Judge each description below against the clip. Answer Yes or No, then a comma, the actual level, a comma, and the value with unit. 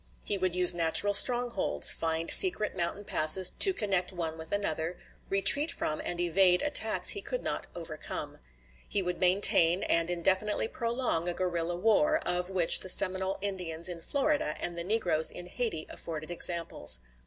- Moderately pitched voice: Yes, medium, 180 Hz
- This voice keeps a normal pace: Yes, average, 160 wpm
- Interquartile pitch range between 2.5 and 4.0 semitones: Yes, average, 3.3 semitones